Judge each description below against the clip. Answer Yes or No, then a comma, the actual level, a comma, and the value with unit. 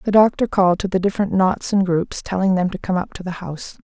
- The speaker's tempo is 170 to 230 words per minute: No, fast, 265 wpm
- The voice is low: No, high, 190 Hz